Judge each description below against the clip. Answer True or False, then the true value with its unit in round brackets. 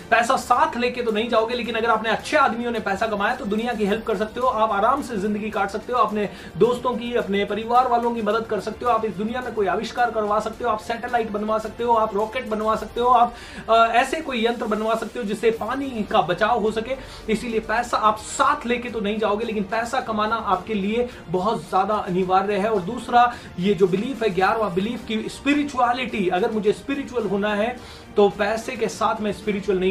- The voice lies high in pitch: True (220 Hz)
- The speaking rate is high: True (220 wpm)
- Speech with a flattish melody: True (2.3 semitones)